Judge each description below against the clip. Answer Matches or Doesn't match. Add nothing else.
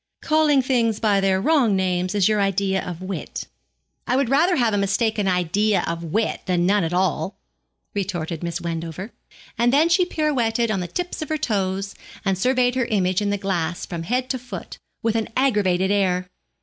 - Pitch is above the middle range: Matches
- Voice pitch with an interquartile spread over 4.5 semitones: Matches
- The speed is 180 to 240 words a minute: Matches